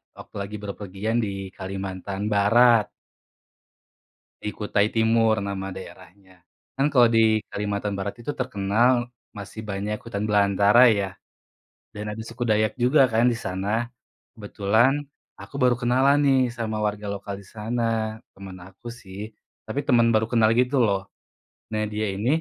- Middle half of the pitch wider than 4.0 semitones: No, average, 2.8 semitones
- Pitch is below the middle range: Yes, low, 105 Hz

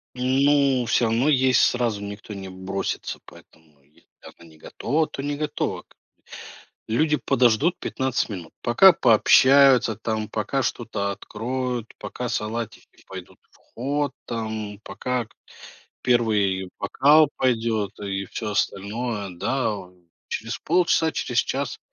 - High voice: No, low, 115 Hz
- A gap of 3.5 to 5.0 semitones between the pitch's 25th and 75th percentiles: Yes, average, 4.3 semitones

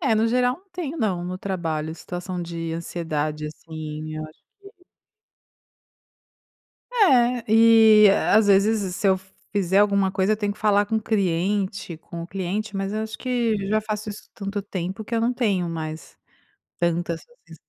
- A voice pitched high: Yes, high, 200 Hz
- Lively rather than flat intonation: No, average, 4.3 semitones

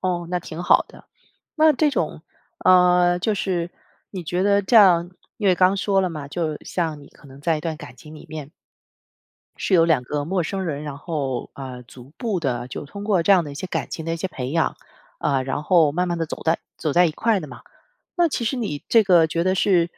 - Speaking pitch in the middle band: Yes, medium, 170 Hz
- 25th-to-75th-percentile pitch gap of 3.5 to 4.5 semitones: Yes, average, 3.9 semitones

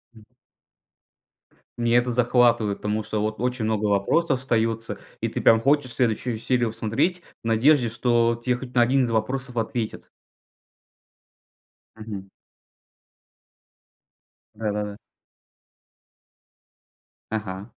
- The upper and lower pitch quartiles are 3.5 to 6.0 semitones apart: No, narrow, 2.4 semitones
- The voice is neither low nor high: No, low, 115 Hz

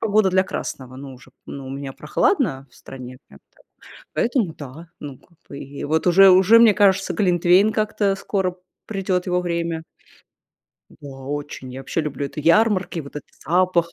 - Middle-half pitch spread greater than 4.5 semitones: Yes, wide, 5.5 semitones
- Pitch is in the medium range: Yes, medium, 170 Hz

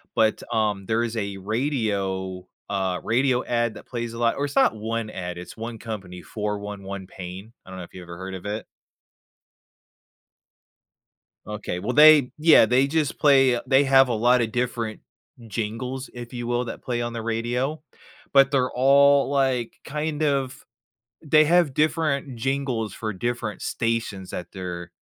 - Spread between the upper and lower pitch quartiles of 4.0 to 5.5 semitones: Yes, average, 4.6 semitones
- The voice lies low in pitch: Yes, low, 115 Hz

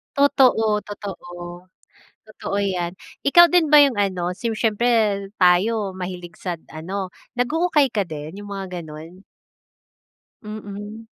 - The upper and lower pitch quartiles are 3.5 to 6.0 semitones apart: Yes, average, 4.2 semitones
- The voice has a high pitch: Yes, high, 205 Hz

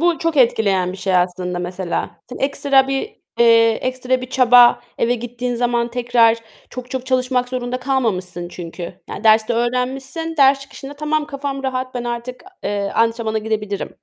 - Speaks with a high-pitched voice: Yes, high, 245 Hz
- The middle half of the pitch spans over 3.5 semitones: No, average, 3.2 semitones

